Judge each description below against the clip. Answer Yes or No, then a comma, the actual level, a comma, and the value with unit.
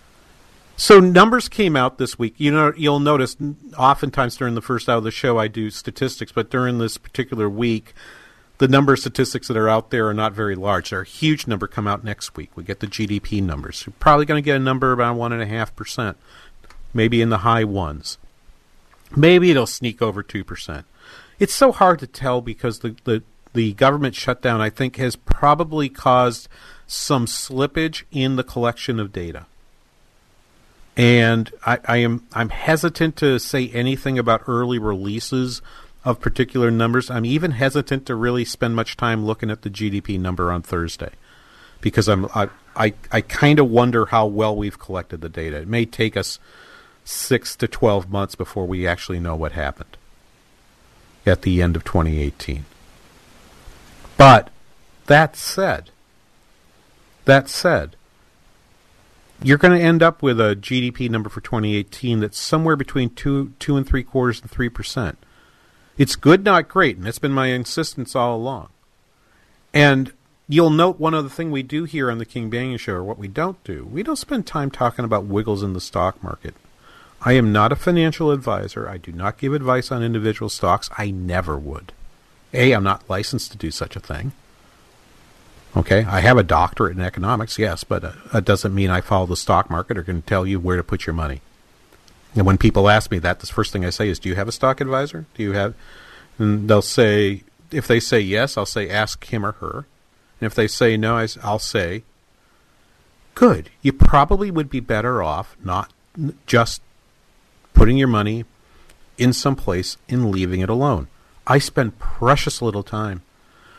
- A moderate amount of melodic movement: Yes, average, 4.7 semitones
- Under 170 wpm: No, average, 180 wpm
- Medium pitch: No, low, 115 Hz